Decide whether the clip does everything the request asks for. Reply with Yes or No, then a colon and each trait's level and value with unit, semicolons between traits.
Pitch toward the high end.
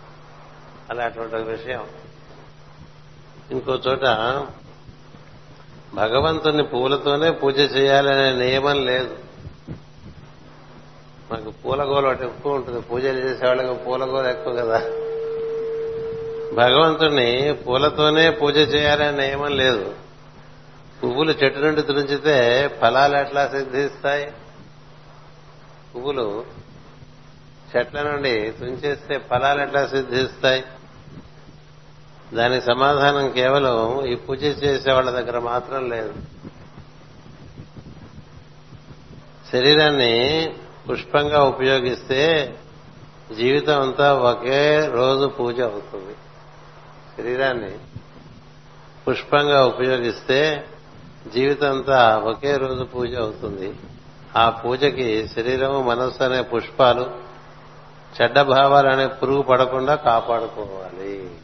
No: low, 135 Hz